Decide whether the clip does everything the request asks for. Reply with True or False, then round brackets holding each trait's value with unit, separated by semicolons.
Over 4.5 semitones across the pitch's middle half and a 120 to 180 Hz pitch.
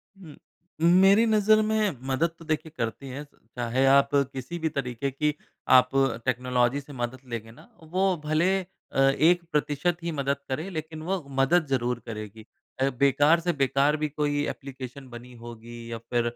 True (4.9 semitones; 140 Hz)